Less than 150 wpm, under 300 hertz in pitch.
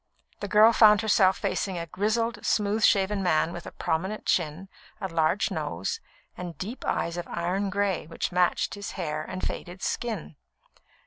No: average, 165 wpm; high, 190 Hz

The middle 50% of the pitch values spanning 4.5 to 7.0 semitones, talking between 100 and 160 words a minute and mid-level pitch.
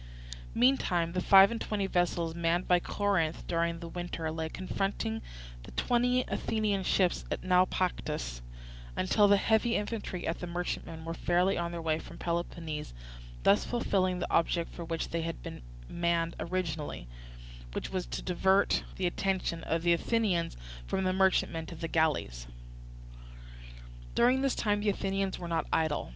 No: average, 2.8 semitones; average, 155 wpm; medium, 175 Hz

